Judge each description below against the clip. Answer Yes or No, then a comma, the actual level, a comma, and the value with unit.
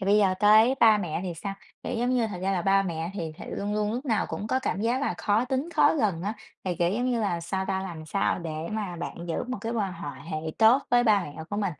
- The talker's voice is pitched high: Yes, high, 205 Hz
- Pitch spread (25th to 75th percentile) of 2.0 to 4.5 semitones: Yes, average, 4.0 semitones